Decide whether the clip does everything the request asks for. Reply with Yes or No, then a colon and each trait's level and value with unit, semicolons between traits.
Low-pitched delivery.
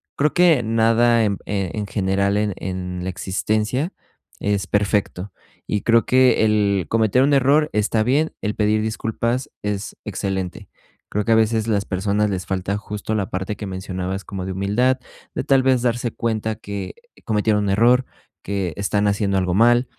Yes: low, 105 Hz